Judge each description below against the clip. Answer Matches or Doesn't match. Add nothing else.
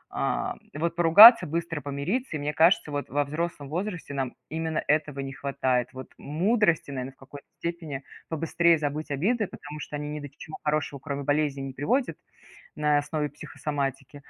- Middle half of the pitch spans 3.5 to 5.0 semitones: Doesn't match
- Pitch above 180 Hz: Doesn't match